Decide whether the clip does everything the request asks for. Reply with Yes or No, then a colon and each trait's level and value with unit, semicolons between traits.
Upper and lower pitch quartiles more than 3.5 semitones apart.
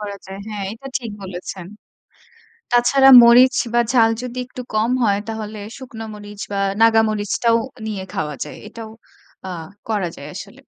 No: average, 2.7 semitones